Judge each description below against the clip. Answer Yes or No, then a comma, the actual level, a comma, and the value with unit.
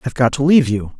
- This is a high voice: No, low, 130 Hz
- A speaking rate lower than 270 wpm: No, fast, 300 wpm